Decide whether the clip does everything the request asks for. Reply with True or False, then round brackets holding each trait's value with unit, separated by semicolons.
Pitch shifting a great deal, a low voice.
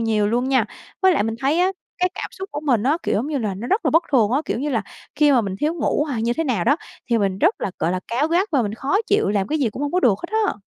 False (6.1 semitones; 265 Hz)